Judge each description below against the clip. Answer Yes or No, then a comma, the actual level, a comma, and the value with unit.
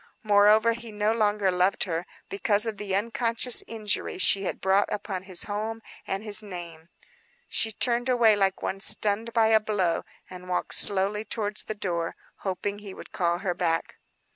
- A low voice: No, high, 205 Hz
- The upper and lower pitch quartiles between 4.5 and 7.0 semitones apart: No, narrow, 2.6 semitones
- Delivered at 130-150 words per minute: No, average, 170 wpm